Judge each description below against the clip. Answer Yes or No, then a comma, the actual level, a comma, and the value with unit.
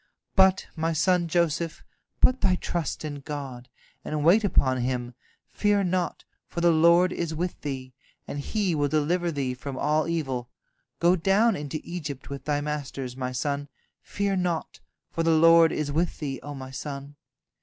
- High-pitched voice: No, medium, 155 Hz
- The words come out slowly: No, average, 165 wpm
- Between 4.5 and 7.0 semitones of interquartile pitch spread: No, average, 3.7 semitones